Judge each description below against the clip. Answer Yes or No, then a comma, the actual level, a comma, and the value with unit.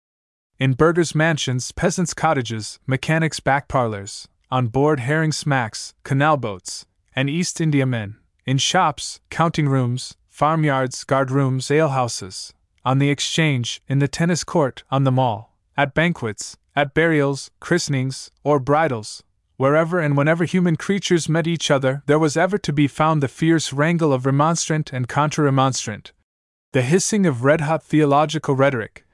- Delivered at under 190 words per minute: Yes, average, 145 wpm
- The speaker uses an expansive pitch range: No, average, 3.6 semitones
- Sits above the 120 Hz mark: Yes, medium, 140 Hz